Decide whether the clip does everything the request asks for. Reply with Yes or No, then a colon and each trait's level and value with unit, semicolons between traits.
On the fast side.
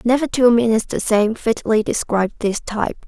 No: average, 175 wpm